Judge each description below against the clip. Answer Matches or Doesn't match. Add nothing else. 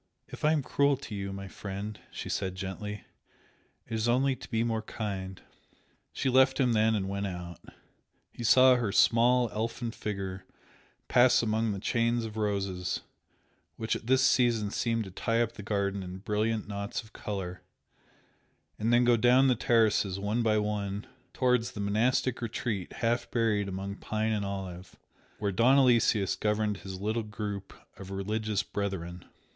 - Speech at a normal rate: Matches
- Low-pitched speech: Matches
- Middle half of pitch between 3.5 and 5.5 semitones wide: Doesn't match